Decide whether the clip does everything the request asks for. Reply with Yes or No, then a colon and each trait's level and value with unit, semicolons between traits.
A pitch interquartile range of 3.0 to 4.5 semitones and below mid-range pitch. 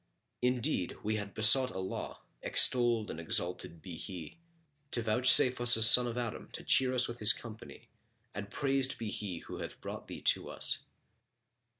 Yes: average, 3.5 semitones; low, 115 Hz